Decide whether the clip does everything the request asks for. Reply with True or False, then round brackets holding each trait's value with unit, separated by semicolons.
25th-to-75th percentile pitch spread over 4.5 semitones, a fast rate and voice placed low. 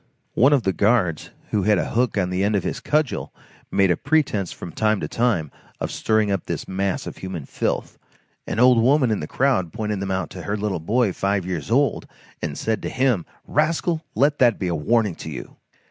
True (4.9 semitones; 215 wpm; 105 Hz)